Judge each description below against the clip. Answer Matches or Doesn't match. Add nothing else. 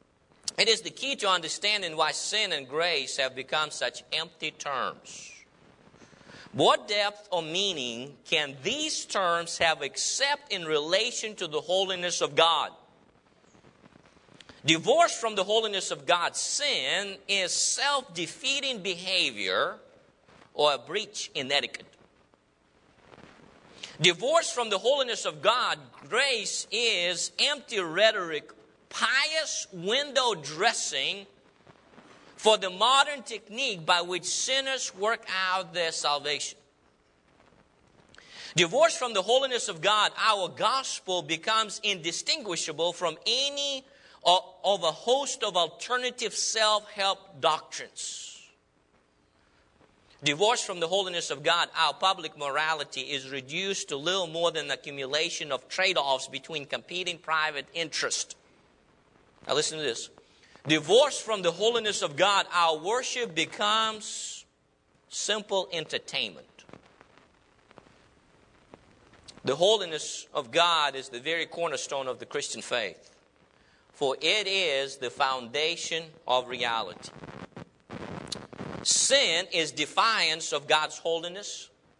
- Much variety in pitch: Matches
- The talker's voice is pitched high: Doesn't match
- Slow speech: Matches